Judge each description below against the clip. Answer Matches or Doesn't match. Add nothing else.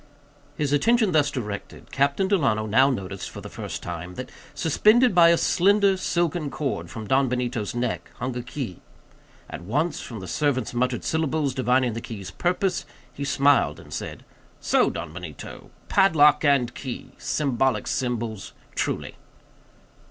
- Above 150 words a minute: Doesn't match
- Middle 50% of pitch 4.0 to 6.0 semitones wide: Matches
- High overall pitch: Doesn't match